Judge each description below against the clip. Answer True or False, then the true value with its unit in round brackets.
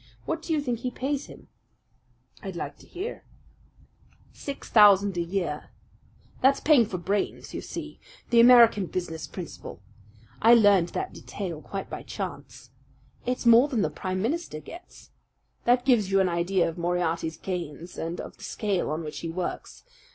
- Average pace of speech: True (165 wpm)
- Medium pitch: False (195 Hz)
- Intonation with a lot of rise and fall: True (5.9 semitones)